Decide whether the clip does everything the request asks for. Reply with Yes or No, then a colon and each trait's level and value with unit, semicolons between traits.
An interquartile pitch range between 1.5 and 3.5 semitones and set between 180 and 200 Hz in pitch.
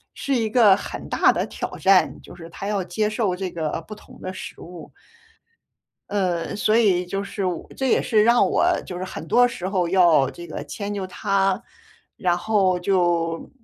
Yes: average, 2.9 semitones; high, 190 Hz